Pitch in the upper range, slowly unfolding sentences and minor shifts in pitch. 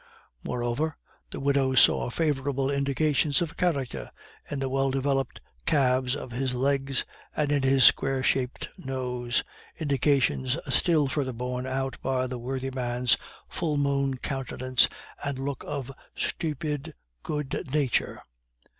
No: low, 135 Hz; slow, 130 wpm; narrow, 1.7 semitones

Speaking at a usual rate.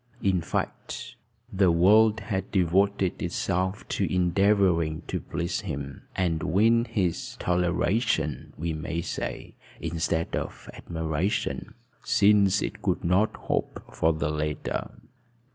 No: slow, 115 wpm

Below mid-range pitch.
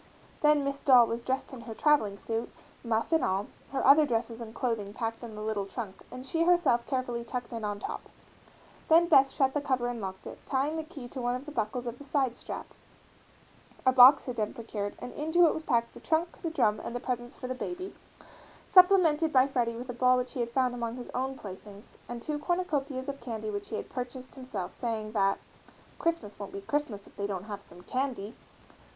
No: high, 245 Hz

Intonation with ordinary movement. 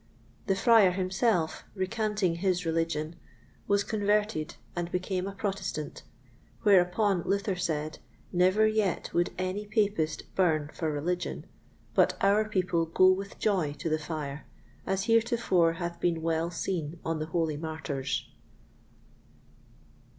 Yes: average, 3.5 semitones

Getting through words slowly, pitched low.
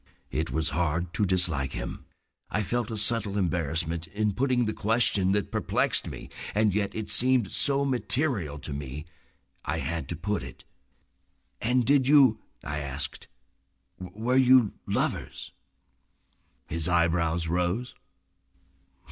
Yes: slow, 130 wpm; very low, 95 Hz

